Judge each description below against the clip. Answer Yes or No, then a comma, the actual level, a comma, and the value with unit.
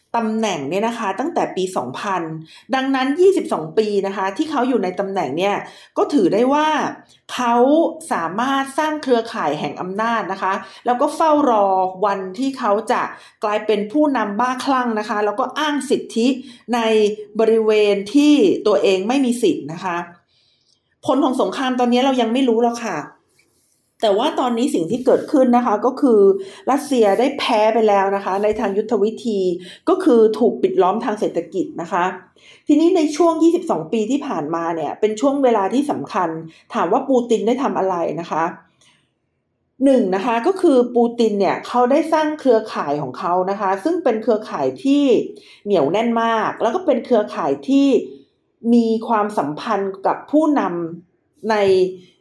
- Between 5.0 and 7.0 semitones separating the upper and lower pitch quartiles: Yes, wide, 5.4 semitones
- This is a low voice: No, high, 225 Hz